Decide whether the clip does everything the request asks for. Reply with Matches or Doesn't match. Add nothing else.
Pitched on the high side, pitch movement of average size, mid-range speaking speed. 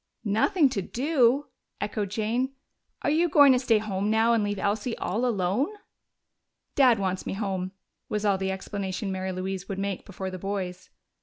Matches